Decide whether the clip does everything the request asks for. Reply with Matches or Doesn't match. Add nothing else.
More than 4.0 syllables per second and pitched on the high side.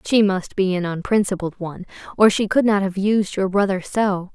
Matches